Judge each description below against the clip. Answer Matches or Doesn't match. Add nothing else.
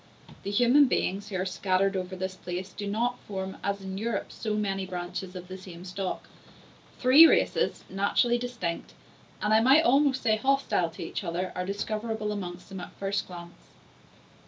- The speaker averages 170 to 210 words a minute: Matches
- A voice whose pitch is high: Matches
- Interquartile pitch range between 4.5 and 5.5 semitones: Doesn't match